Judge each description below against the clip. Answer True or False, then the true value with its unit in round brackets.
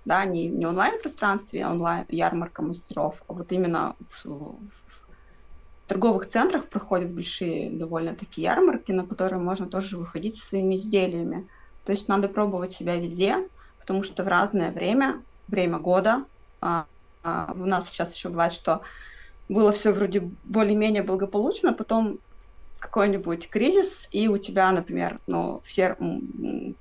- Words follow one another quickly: False (140 wpm)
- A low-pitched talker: False (190 Hz)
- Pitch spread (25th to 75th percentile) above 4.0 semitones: False (3.2 semitones)